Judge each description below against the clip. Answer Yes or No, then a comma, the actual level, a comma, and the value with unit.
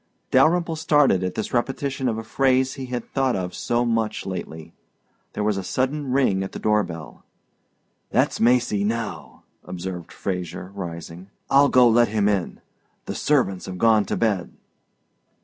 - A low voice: Yes, low, 110 Hz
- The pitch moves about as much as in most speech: No, wide, 5.7 semitones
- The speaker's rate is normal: Yes, average, 160 wpm